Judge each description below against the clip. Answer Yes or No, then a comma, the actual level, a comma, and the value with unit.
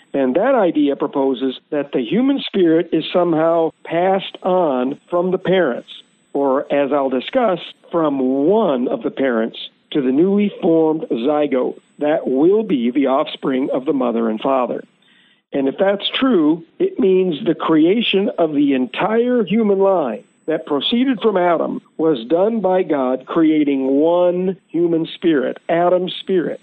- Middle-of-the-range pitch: Yes, medium, 170 Hz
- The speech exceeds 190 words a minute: No, average, 150 wpm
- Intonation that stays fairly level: No, average, 5.1 semitones